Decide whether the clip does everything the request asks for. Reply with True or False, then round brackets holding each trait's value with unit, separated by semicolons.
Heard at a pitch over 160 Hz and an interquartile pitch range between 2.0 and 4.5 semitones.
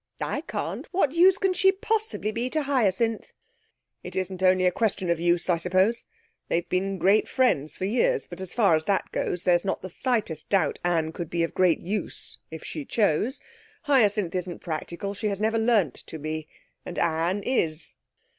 False (190 Hz; 5.2 semitones)